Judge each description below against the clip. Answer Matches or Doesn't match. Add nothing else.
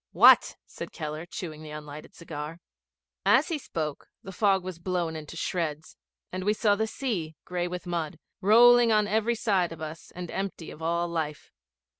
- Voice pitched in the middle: Matches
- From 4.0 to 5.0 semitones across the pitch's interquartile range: Matches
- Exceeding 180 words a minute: Doesn't match